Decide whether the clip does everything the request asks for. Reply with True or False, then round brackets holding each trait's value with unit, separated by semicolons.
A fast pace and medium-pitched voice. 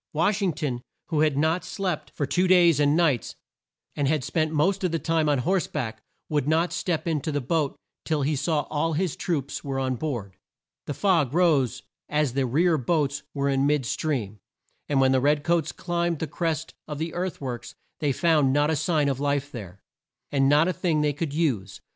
True (215 wpm; 150 Hz)